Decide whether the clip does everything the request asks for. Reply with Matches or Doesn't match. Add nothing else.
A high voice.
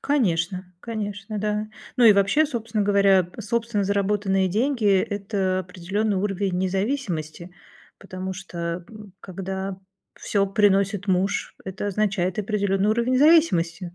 Matches